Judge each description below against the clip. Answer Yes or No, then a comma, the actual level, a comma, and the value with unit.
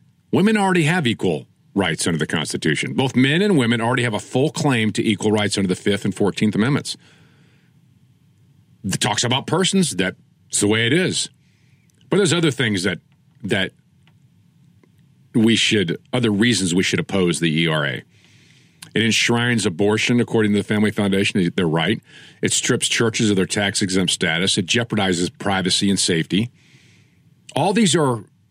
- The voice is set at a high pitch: No, low, 110 Hz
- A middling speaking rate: Yes, average, 160 wpm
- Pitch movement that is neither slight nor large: No, wide, 5.8 semitones